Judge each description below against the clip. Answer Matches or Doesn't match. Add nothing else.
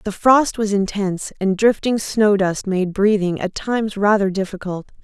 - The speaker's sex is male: Doesn't match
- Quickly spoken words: Doesn't match